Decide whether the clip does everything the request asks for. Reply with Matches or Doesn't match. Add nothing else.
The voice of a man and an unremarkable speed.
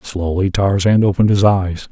Matches